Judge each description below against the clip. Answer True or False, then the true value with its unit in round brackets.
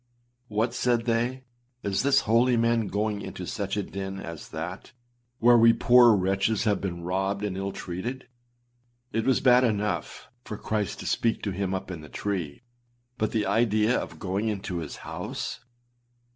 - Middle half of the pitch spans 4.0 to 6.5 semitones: False (3.3 semitones)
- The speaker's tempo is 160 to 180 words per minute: True (170 wpm)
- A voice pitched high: False (105 Hz)